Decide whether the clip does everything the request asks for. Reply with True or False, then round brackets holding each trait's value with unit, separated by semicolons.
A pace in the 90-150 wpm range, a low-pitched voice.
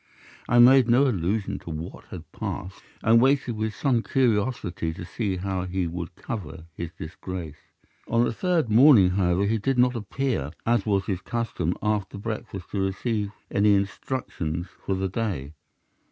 False (160 wpm; 100 Hz)